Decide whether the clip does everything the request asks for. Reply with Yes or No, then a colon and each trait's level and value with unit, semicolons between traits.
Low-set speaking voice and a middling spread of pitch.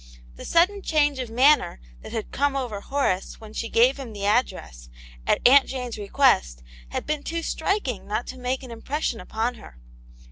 No: very high, 250 Hz; average, 4.8 semitones